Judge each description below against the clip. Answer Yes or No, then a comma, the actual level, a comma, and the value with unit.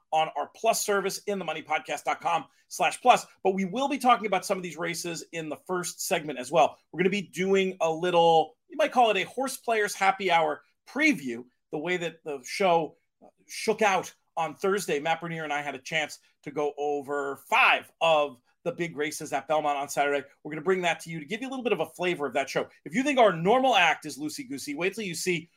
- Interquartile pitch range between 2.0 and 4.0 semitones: No, average, 4.9 semitones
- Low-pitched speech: No, medium, 170 Hz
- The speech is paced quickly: Yes, fast, 240 wpm